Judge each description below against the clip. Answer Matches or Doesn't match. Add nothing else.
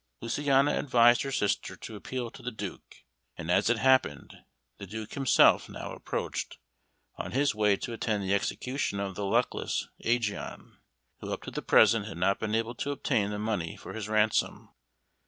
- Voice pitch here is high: Doesn't match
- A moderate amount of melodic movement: Matches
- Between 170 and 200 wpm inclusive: Matches